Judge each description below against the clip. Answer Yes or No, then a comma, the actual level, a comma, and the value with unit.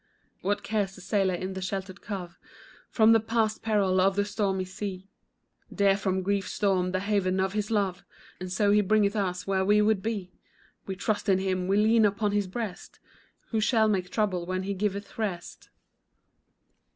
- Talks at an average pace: Yes, average, 180 wpm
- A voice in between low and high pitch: No, high, 200 Hz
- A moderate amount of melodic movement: No, narrow, 2.0 semitones